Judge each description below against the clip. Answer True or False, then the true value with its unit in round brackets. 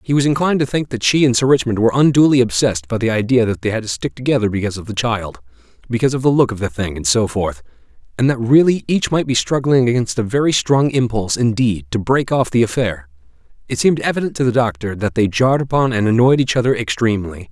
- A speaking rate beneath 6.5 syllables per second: False (6.6 syllables/s)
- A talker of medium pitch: False (115 Hz)